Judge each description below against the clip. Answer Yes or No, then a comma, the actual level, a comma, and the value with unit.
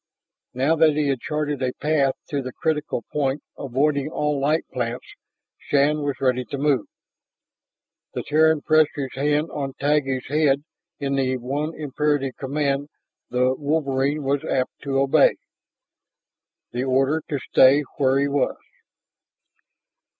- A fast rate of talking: No, slow, 135 wpm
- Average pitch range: No, narrow, 2.0 semitones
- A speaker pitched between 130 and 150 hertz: Yes, medium, 140 Hz